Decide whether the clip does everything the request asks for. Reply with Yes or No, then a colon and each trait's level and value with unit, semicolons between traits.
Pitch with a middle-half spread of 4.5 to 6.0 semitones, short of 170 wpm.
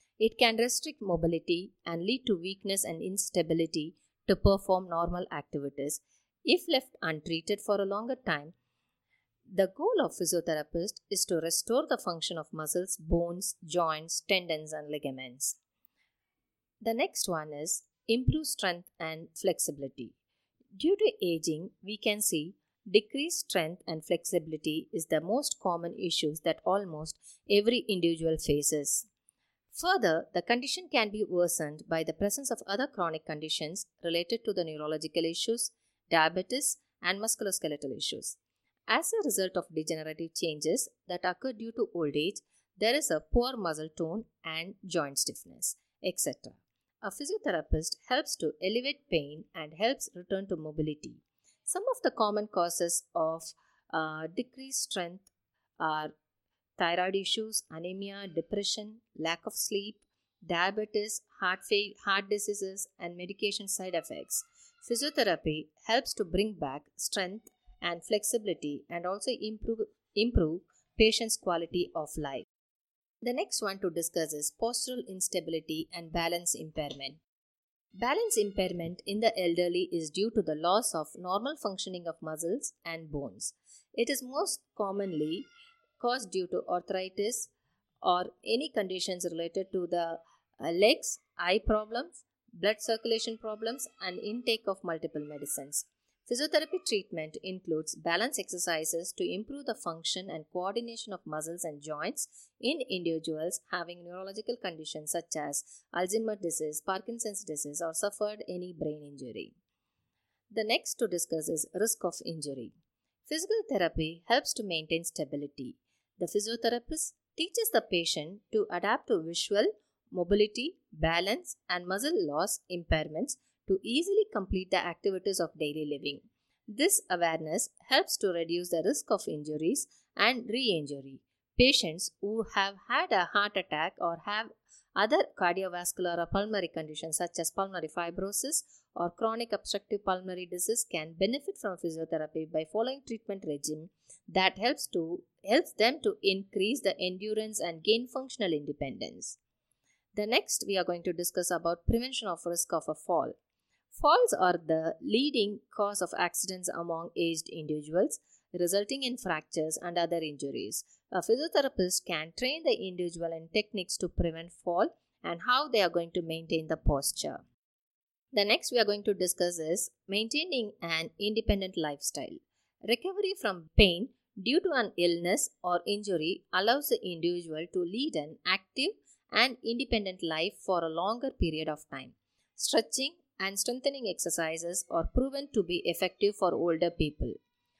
Yes: average, 5.1 semitones; average, 140 wpm